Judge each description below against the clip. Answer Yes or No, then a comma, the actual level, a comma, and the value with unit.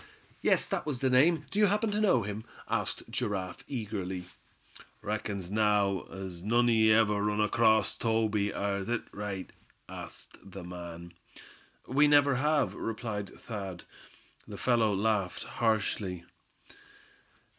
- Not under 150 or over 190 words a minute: No, slow, 135 wpm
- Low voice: Yes, low, 105 Hz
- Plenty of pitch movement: No, average, 3.6 semitones